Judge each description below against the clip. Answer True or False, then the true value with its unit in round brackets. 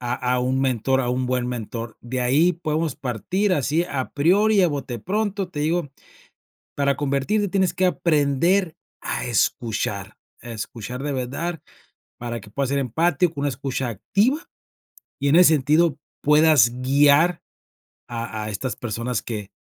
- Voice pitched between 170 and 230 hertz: False (140 Hz)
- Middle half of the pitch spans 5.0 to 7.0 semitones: True (5.3 semitones)